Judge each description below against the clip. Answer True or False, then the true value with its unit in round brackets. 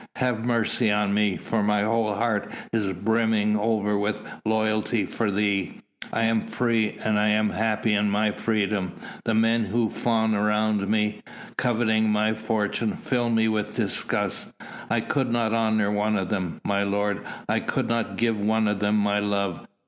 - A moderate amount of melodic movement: False (1.4 semitones)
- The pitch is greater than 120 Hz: False (110 Hz)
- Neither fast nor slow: True (165 wpm)